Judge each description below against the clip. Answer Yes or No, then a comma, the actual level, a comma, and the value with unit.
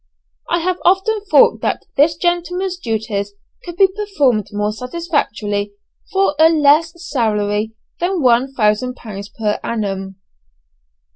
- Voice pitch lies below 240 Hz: No, very high, 265 Hz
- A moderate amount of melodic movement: No, wide, 8.7 semitones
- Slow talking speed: Yes, slow, 125 wpm